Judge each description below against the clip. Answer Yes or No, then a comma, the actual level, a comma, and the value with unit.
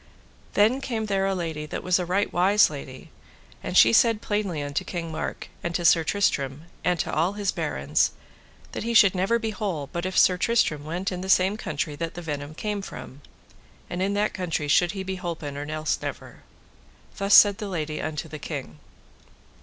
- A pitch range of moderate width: Yes, average, 4.6 semitones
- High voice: No, medium, 180 Hz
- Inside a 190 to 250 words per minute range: Yes, average, 200 wpm